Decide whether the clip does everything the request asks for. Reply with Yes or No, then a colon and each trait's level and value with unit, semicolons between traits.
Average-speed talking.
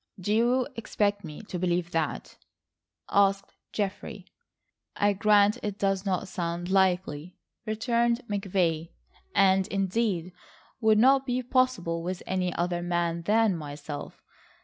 No: slow, 125 wpm